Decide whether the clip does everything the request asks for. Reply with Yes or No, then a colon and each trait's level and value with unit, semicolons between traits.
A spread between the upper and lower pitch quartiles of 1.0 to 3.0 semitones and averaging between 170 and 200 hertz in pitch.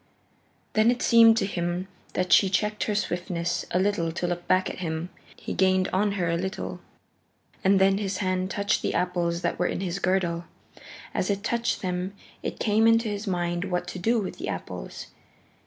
Yes: narrow, 2.5 semitones; medium, 185 Hz